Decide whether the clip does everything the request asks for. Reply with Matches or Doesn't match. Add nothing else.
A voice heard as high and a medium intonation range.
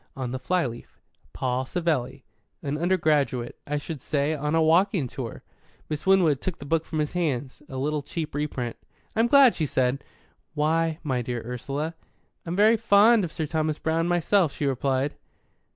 Doesn't match